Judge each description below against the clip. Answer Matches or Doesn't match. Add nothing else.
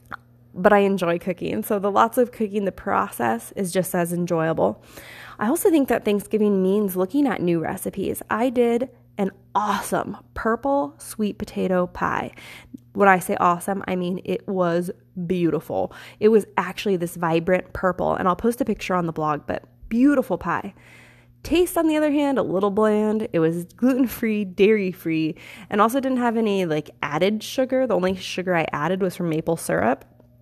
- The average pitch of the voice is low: Doesn't match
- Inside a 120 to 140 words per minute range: Doesn't match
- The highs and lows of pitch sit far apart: Doesn't match